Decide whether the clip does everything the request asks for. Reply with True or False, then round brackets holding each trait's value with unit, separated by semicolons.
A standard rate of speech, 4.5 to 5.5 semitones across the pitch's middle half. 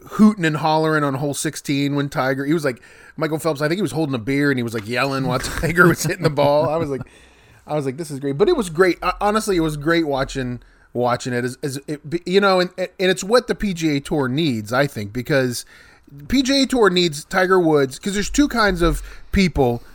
False (235 wpm; 4.9 semitones)